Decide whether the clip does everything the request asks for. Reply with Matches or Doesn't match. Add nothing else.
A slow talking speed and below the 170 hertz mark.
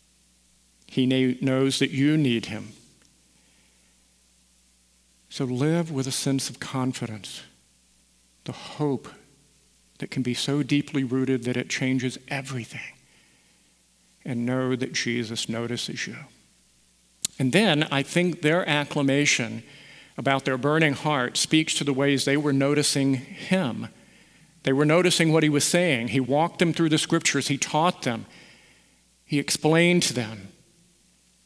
Matches